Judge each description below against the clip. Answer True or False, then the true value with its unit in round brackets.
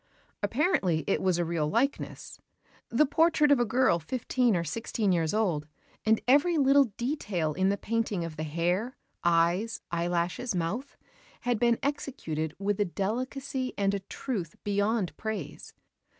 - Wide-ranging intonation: True (6.6 semitones)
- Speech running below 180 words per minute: True (150 wpm)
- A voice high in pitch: True (205 Hz)